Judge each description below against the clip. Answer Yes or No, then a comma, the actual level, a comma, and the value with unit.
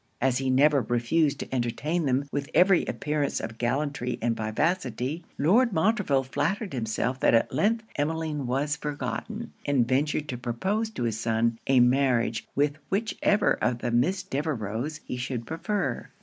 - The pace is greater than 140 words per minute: Yes, average, 155 wpm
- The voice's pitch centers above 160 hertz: No, medium, 140 Hz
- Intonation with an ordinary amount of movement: Yes, average, 4.9 semitones